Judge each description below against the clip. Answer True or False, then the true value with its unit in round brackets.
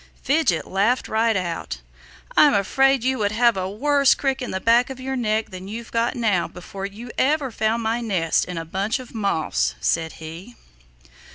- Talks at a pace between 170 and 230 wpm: True (185 wpm)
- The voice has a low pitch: False (220 Hz)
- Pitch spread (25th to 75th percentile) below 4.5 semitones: False (5.1 semitones)